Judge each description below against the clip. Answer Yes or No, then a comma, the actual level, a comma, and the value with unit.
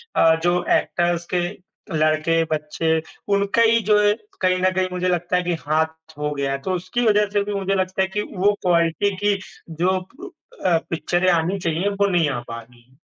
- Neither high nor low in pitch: Yes, medium, 180 Hz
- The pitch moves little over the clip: No, average, 3.5 semitones